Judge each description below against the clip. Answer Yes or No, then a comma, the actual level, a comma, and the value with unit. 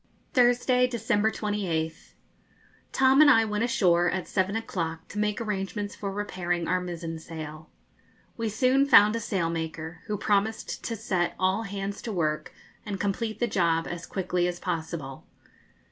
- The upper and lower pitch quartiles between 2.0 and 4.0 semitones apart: No, average, 4.5 semitones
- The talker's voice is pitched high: Yes, high, 195 Hz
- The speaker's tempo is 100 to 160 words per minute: Yes, average, 150 wpm